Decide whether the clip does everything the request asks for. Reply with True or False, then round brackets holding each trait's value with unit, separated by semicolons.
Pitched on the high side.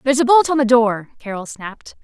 True (245 Hz)